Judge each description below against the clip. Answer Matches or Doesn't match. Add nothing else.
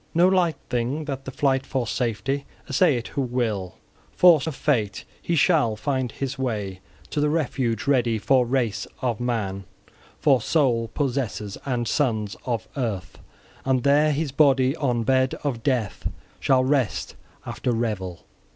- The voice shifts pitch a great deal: Doesn't match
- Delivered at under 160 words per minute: Matches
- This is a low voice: Matches